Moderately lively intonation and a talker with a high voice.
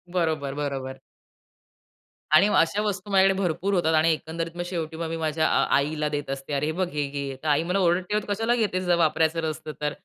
No: average, 3.4 semitones; medium, 160 Hz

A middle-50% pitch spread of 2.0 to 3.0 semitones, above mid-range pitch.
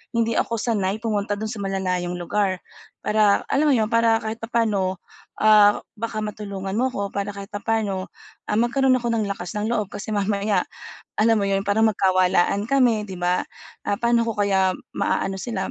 Yes: narrow, 2.4 semitones; high, 210 Hz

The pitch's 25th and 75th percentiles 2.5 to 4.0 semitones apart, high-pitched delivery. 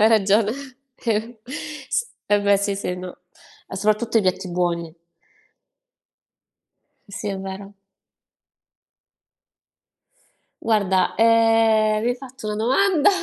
Yes: average, 2.8 semitones; high, 215 Hz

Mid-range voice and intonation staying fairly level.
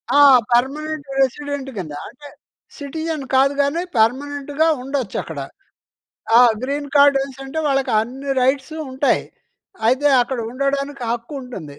No: very high, 275 Hz; narrow, 2.1 semitones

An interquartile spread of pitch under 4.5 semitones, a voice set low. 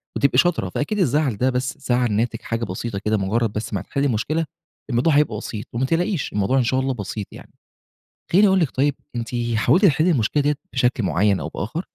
No: wide, 5.4 semitones; low, 125 Hz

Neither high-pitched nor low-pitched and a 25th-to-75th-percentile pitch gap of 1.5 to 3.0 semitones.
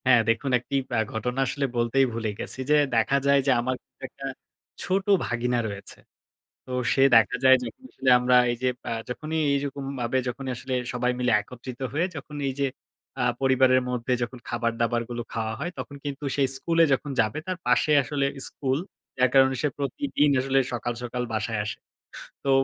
No: low, 130 Hz; narrow, 2.6 semitones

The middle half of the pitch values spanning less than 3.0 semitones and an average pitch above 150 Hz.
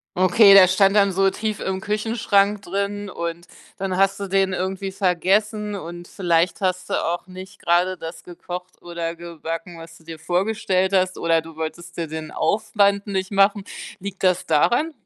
Yes: narrow, 2.6 semitones; medium, 185 Hz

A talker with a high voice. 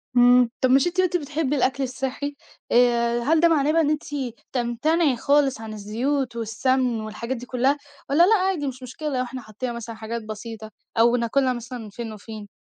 Yes: very high, 250 Hz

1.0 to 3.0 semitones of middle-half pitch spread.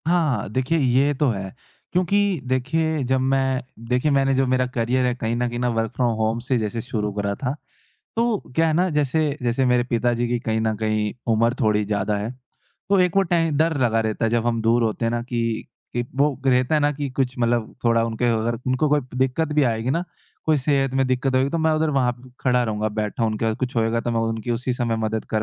No: average, 3.4 semitones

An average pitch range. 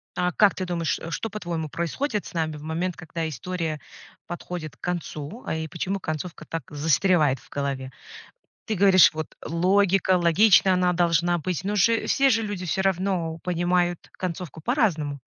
Yes: average, 3.1 semitones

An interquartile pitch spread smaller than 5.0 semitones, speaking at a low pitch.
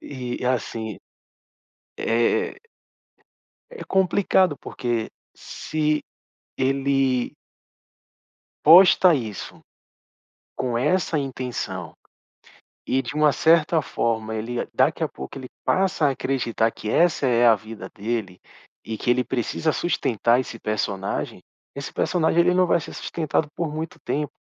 No: average, 5.3 semitones; low, 130 Hz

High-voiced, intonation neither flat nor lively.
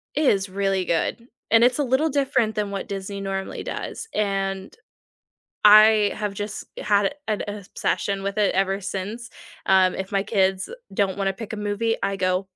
No: high, 200 Hz; narrow, 1.9 semitones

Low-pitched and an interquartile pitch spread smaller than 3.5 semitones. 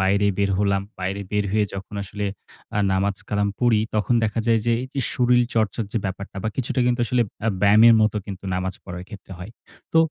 Yes: low, 105 Hz; average, 2.9 semitones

